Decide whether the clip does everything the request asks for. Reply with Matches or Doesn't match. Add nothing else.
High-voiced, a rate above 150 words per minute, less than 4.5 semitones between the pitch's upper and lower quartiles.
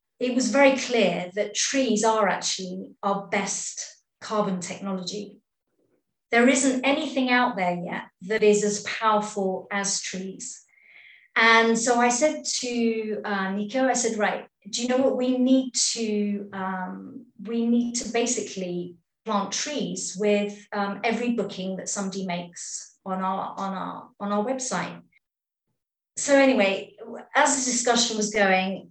Doesn't match